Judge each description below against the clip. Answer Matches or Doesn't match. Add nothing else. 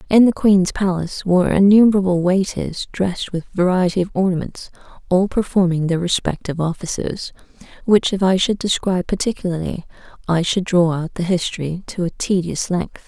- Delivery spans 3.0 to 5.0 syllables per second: Doesn't match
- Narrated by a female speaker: Matches